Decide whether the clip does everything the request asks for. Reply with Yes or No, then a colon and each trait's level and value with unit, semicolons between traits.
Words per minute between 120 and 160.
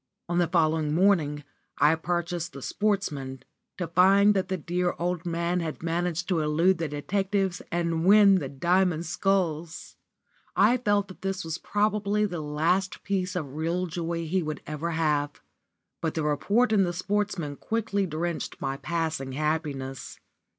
Yes: average, 155 wpm